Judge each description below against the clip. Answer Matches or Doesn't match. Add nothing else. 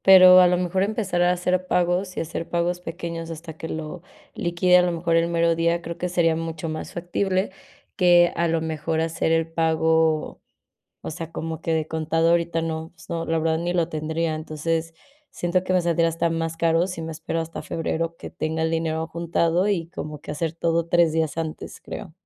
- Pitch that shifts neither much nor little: Doesn't match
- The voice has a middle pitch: Matches